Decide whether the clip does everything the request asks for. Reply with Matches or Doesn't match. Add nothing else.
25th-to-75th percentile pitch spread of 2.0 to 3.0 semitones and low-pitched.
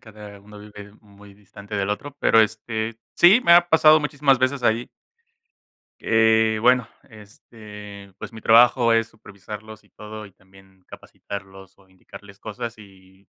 Matches